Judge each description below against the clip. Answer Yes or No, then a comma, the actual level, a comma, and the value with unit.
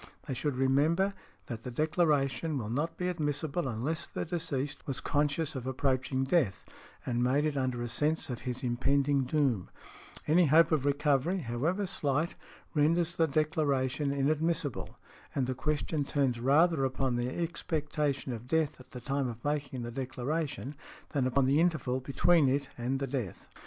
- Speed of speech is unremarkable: Yes, average, 160 wpm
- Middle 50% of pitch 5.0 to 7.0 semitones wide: No, average, 3.3 semitones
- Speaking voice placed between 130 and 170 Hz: Yes, medium, 140 Hz